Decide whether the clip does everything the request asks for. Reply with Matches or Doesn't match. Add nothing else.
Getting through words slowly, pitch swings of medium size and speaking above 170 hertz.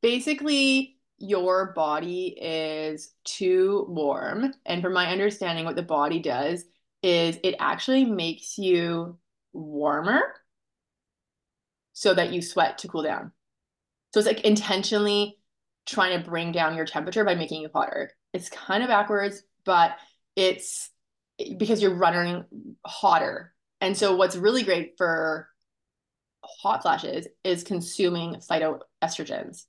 Matches